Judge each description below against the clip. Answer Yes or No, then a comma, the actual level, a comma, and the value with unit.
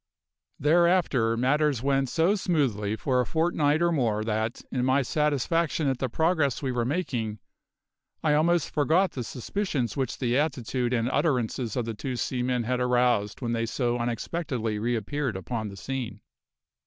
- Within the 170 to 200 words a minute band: No, average, 155 wpm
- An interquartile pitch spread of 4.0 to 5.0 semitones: Yes, average, 4.3 semitones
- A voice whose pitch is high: No, low, 130 Hz